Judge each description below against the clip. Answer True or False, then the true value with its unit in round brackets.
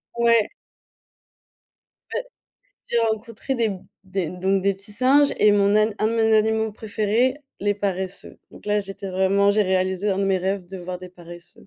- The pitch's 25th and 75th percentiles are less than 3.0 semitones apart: True (2.6 semitones)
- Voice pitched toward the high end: True (200 Hz)